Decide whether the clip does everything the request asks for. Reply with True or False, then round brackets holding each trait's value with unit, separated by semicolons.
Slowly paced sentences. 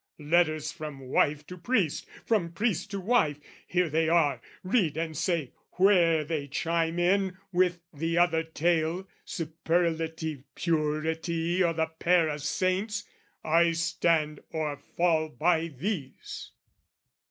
True (125 wpm)